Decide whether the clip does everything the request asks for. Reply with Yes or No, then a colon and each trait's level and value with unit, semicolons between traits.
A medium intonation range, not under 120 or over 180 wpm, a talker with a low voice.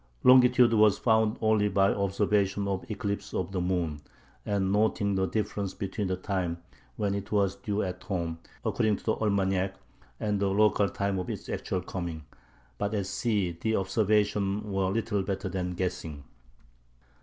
No: narrow, 2.0 semitones; average, 160 wpm; low, 100 Hz